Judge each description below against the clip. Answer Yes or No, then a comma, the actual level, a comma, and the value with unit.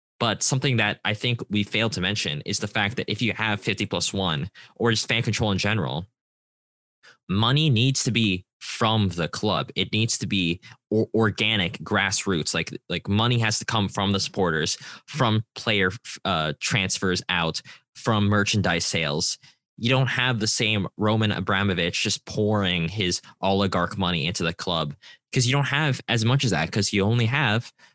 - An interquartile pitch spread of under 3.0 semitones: No, average, 3.3 semitones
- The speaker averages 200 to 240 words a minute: No, average, 175 wpm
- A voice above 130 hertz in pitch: No, low, 105 Hz